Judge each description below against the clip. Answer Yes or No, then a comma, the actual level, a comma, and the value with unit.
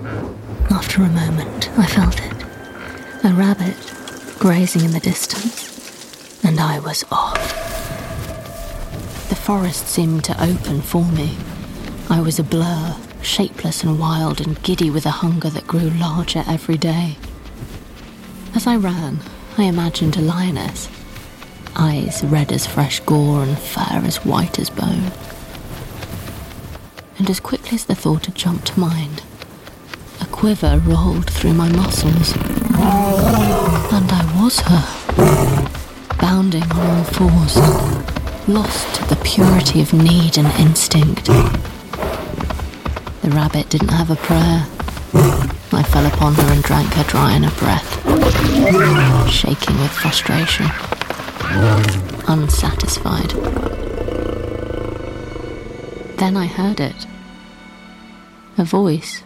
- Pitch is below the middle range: No, medium, 165 Hz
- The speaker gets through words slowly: Yes, slow, 115 wpm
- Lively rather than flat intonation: No, average, 4.1 semitones